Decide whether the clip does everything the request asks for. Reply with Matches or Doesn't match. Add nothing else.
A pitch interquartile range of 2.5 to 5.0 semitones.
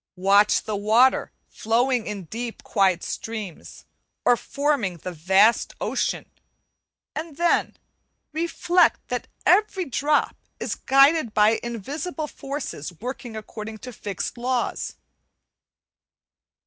Doesn't match